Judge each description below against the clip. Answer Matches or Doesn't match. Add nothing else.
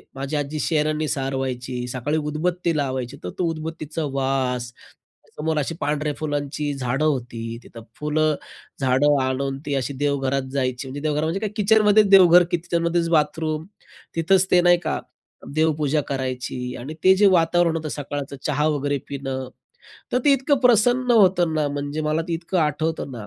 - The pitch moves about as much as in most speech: Matches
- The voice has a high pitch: Doesn't match